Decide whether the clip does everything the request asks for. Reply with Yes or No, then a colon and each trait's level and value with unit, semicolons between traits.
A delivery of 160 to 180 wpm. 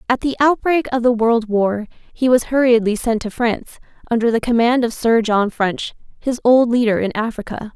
No: average, 195 wpm